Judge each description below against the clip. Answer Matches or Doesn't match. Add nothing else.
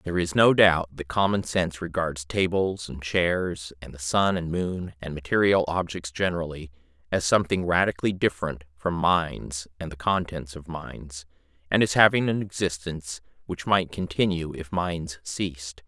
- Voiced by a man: Matches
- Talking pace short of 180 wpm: Matches